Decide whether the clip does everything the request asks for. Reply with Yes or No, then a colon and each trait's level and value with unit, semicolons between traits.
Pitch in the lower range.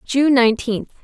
No: very high, 250 Hz